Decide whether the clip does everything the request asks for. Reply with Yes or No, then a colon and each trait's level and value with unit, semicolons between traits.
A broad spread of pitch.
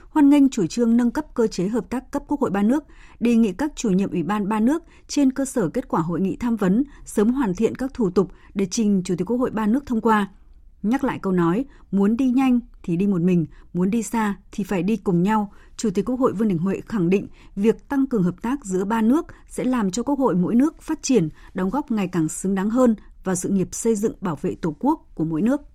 No: average, 4.8 semitones